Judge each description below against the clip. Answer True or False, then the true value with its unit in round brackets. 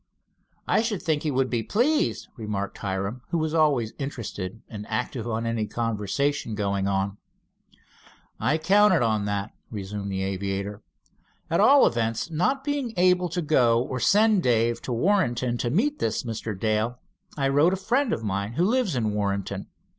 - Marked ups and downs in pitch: True (8.3 semitones)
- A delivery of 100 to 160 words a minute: False (170 wpm)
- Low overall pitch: True (120 Hz)